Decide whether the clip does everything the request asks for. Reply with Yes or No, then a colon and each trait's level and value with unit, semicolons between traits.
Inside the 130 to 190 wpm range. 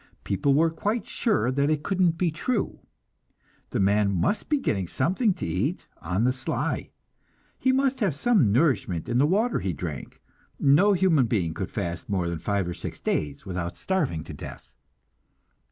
Yes: average, 170 wpm